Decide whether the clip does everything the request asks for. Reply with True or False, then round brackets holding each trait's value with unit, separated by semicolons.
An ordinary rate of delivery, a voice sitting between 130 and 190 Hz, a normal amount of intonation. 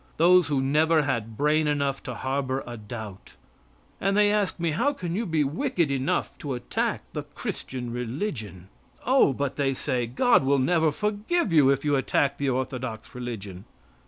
True (170 wpm; 140 Hz; 5.0 semitones)